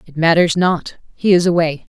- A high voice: No, medium, 170 Hz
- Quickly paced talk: No, average, 150 wpm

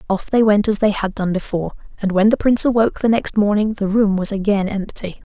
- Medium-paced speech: No, fast, 240 wpm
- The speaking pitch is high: Yes, high, 205 Hz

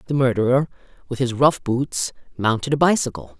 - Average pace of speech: Yes, average, 160 wpm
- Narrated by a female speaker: Yes, female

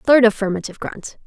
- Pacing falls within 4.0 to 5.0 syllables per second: No, 6.4 syllables/s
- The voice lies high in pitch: Yes, high, 220 Hz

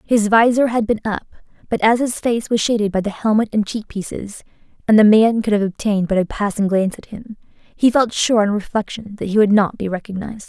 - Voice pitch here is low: No, high, 215 Hz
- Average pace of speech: No, fast, 230 wpm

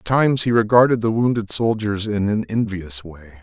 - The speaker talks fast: No, average, 195 wpm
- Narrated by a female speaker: No, male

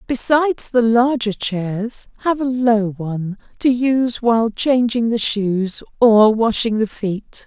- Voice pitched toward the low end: No, high, 230 Hz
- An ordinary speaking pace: Yes, average, 145 wpm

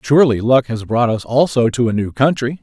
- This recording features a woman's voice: No, male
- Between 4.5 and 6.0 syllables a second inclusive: Yes, 5.6 syllables/s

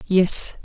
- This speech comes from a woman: Yes, female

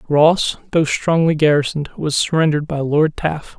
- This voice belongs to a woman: No, male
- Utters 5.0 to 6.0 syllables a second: Yes, 5.6 syllables/s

